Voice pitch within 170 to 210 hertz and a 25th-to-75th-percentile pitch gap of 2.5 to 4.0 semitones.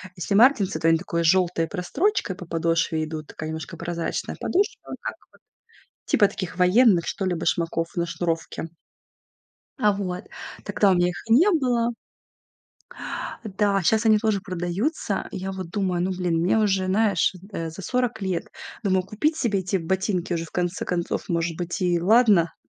Yes: medium, 185 Hz; average, 3.5 semitones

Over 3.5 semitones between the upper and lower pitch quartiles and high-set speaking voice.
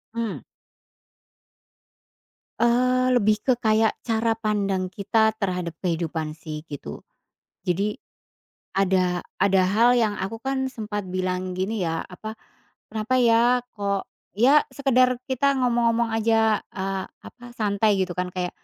Yes: average, 3.9 semitones; high, 215 Hz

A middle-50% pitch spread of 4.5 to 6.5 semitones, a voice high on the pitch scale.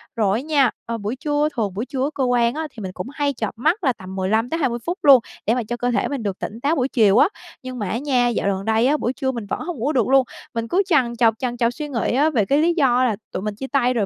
No: average, 3.9 semitones; high, 245 Hz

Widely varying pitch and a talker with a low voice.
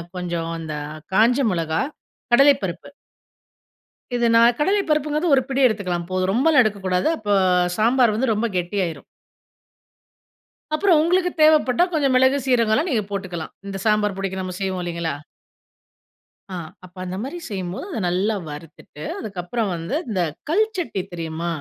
No: wide, 6.6 semitones; high, 205 Hz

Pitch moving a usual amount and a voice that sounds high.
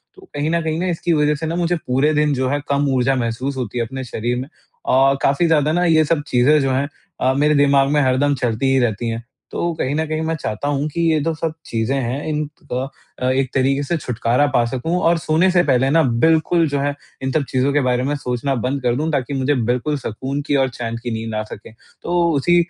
No: average, 3.4 semitones; medium, 140 Hz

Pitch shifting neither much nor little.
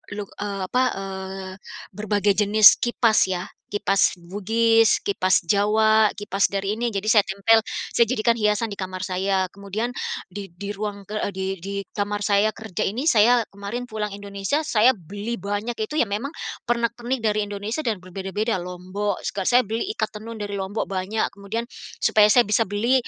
No: narrow, 2.2 semitones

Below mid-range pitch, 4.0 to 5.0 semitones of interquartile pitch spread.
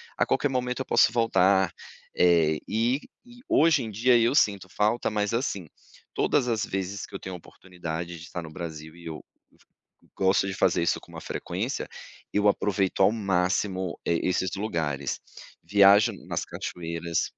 Yes: very low, 95 Hz; average, 4.4 semitones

